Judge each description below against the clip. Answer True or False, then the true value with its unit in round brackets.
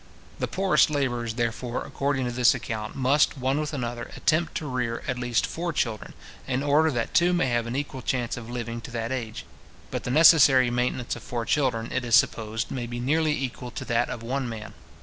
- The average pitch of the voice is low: True (125 Hz)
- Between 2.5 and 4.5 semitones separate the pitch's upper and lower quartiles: True (2.9 semitones)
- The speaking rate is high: True (210 wpm)